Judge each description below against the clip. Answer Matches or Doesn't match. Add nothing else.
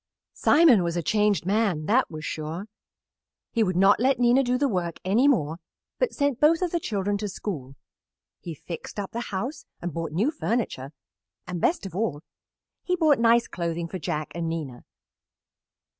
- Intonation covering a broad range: Matches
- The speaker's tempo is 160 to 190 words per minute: Matches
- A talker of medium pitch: Doesn't match